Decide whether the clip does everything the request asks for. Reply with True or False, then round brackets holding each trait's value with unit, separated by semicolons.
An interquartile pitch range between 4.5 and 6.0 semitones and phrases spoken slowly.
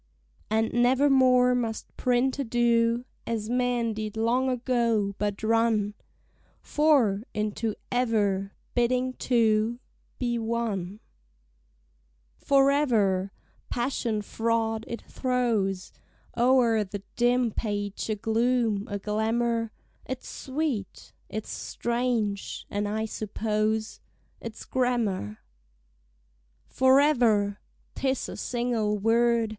False (2.6 semitones; 95 wpm)